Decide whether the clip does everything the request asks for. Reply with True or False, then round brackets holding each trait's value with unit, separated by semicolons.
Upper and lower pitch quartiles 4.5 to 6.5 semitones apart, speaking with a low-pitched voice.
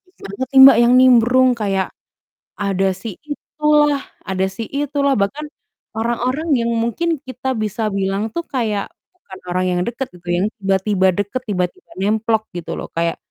False (5.1 semitones; 225 Hz)